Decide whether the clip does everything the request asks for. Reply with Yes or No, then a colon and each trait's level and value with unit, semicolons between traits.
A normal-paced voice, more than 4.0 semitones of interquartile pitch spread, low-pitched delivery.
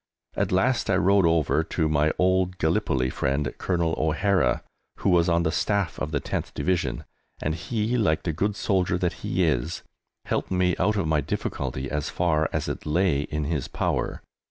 No: average, 180 wpm; average, 3.5 semitones; very low, 85 Hz